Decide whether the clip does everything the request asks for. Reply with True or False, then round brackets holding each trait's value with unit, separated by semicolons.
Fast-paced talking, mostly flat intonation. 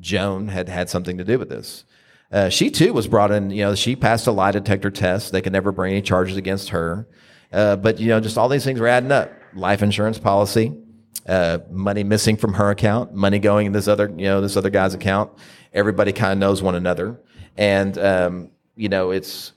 True (220 wpm; 2.0 semitones)